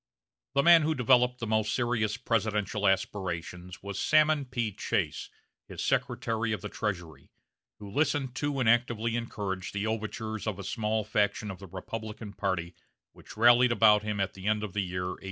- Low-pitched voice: Yes, low, 110 Hz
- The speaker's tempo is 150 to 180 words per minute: Yes, average, 175 wpm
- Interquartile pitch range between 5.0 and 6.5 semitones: No, average, 3.2 semitones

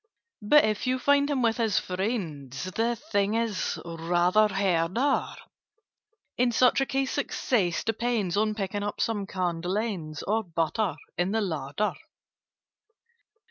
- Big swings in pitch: No, average, 4.7 semitones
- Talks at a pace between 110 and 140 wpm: Yes, slow, 135 wpm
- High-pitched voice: Yes, high, 205 Hz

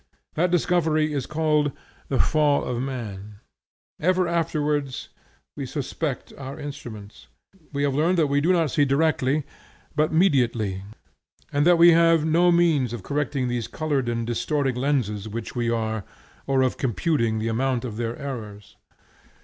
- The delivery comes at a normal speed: Yes, average, 150 wpm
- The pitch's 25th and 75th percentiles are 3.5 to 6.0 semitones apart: Yes, average, 4.7 semitones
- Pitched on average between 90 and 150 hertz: Yes, medium, 140 Hz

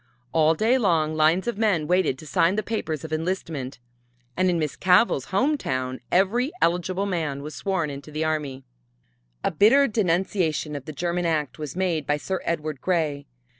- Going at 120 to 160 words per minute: No, average, 175 wpm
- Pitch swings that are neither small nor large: Yes, average, 3.7 semitones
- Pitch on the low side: No, medium, 165 Hz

